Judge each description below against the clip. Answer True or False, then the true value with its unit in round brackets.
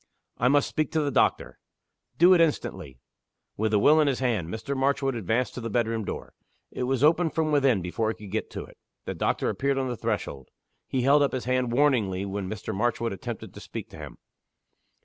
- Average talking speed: False (210 wpm)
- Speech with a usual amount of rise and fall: True (4.6 semitones)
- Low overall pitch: True (125 Hz)